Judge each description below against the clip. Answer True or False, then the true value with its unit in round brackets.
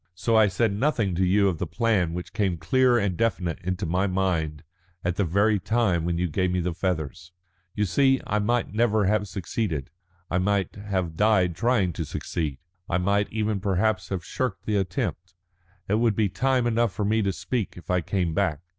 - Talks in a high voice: False (95 Hz)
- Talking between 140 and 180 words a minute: False (200 wpm)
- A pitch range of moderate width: True (3.6 semitones)